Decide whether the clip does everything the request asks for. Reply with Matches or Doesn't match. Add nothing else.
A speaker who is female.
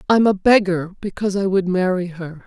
Matches